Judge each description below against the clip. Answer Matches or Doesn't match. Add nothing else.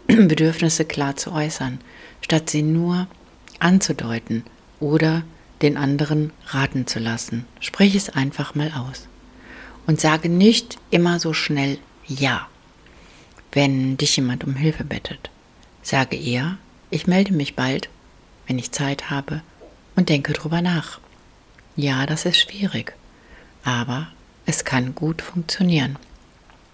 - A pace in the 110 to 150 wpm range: Matches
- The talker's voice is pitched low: Doesn't match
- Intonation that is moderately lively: Matches